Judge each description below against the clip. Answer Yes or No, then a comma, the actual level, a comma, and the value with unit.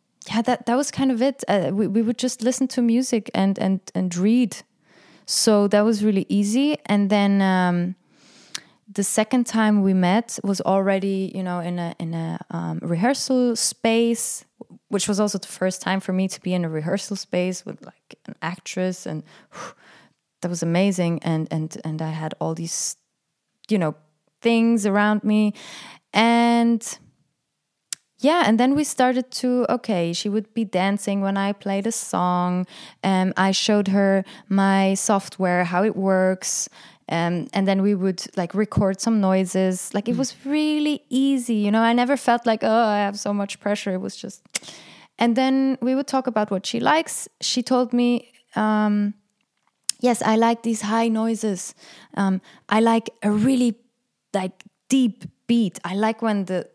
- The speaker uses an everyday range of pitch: Yes, average, 3.6 semitones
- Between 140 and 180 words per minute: Yes, average, 175 wpm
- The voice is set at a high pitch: Yes, high, 205 Hz